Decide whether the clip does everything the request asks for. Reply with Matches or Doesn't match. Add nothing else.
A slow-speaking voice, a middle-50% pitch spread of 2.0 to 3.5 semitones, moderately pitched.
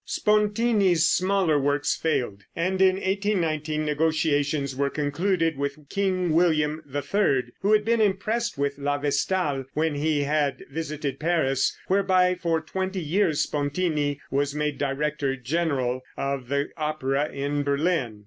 Doesn't match